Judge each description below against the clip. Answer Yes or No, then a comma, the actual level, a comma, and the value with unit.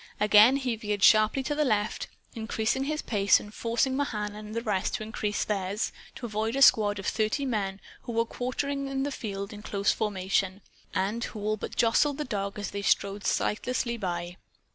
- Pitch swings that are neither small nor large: Yes, average, 3.3 semitones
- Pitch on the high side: Yes, high, 215 Hz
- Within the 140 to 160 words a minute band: No, average, 185 wpm